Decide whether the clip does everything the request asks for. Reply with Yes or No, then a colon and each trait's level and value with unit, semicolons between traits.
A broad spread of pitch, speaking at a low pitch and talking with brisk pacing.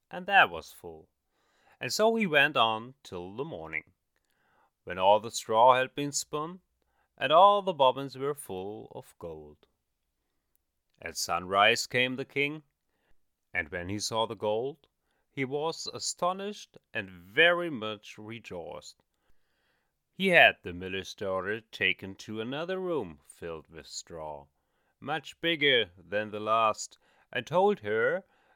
No: wide, 8.5 semitones; low, 115 Hz; slow, 135 wpm